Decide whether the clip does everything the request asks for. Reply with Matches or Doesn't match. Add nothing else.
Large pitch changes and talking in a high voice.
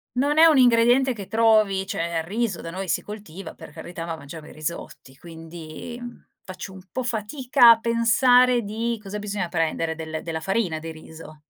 Matches